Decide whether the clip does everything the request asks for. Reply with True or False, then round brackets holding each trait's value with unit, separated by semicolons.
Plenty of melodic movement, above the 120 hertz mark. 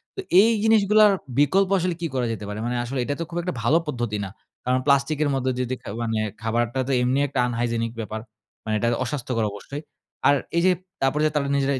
False (4.5 semitones; 135 Hz)